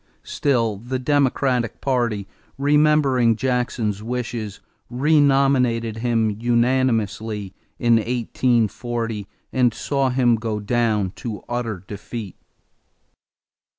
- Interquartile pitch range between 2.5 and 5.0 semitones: Yes, average, 2.8 semitones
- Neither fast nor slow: No, slow, 85 wpm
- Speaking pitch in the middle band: No, low, 120 Hz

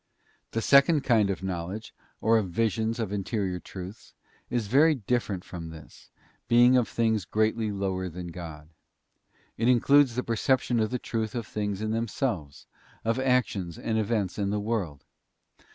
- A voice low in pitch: Yes, low, 110 Hz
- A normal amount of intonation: Yes, average, 3.9 semitones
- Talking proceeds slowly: No, average, 155 wpm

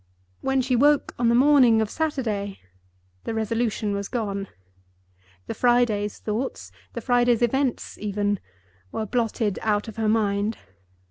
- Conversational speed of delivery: No, slow, 125 wpm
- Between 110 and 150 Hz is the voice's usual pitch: No, high, 220 Hz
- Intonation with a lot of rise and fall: No, average, 3.2 semitones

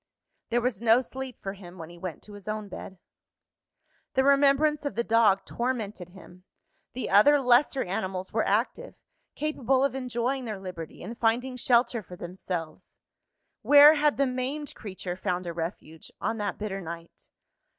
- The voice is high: Yes, high, 225 Hz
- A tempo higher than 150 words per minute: Yes, average, 160 wpm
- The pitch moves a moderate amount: No, wide, 5.7 semitones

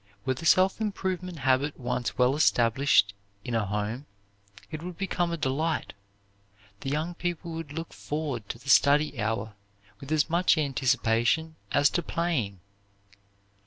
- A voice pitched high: No, medium, 145 Hz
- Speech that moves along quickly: No, average, 145 wpm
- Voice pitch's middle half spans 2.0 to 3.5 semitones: No, average, 5.1 semitones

